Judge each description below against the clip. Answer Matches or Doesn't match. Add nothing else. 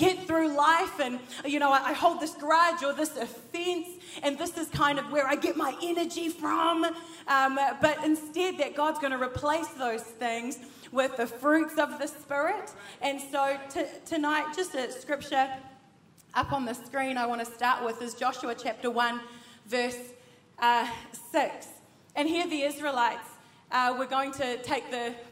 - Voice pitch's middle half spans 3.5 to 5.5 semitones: Matches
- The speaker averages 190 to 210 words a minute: Doesn't match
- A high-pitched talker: Matches